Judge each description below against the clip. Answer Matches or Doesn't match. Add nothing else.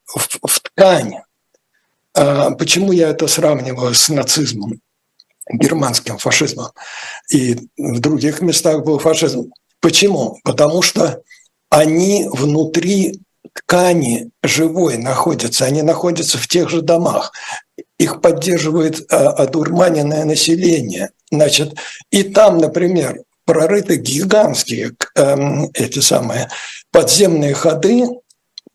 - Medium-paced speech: Doesn't match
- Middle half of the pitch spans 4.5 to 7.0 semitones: Doesn't match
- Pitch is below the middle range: Doesn't match